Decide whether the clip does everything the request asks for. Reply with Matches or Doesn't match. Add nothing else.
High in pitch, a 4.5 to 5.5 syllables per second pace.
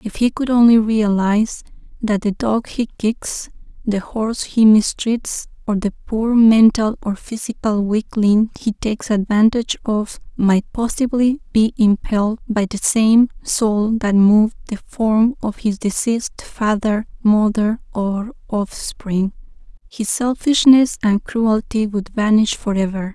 Doesn't match